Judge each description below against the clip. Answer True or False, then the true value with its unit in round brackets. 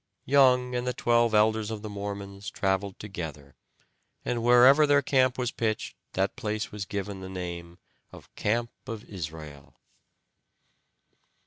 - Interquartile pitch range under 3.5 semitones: False (4.2 semitones)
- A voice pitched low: True (105 Hz)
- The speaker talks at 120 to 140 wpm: True (135 wpm)